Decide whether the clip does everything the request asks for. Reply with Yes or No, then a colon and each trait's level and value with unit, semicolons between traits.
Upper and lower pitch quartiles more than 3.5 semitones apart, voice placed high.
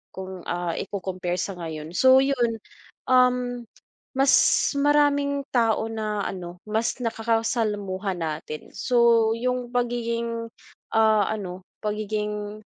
Yes: average, 4.2 semitones; high, 220 Hz